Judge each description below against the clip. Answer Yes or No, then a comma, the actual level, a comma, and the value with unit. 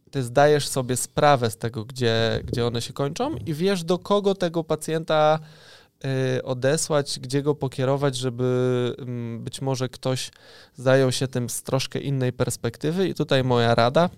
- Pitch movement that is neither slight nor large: Yes, average, 3.2 semitones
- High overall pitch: No, low, 135 Hz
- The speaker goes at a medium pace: Yes, average, 150 wpm